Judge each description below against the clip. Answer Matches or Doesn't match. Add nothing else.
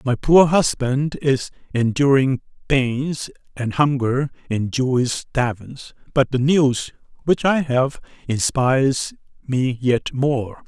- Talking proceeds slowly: Matches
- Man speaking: Matches